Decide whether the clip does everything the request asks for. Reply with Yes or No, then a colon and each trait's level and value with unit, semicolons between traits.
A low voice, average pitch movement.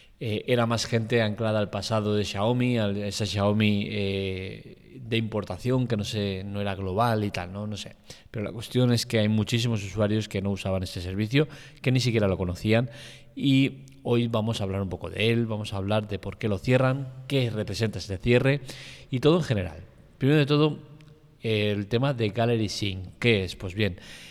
Yes: low, 110 Hz; average, 3.4 semitones